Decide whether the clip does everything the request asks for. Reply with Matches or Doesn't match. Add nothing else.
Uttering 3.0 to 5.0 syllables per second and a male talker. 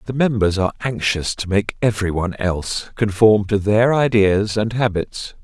Matches